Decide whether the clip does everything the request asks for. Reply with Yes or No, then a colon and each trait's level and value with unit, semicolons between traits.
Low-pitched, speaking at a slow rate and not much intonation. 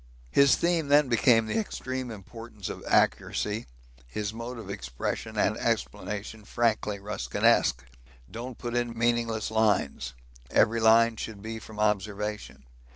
Yes: low, 110 Hz; slow, 130 wpm; narrow, 2.2 semitones